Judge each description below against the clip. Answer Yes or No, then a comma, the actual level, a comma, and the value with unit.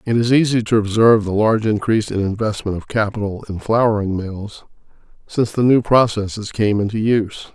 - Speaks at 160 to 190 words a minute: Yes, average, 175 wpm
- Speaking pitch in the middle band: No, low, 110 Hz